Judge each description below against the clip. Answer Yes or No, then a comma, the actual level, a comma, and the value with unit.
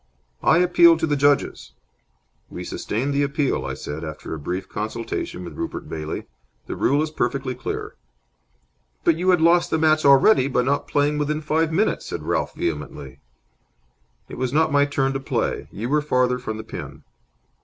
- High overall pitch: No, medium, 140 Hz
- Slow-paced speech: No, average, 175 wpm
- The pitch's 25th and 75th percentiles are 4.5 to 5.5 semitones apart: Yes, average, 5.0 semitones